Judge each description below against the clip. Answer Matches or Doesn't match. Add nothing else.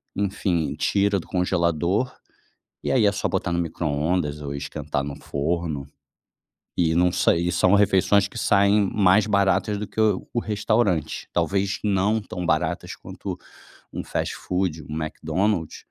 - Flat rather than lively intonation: Doesn't match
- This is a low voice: Matches